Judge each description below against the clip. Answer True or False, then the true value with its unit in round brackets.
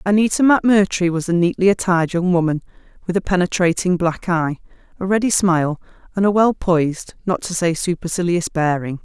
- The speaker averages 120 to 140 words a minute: False (165 wpm)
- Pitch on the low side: False (180 Hz)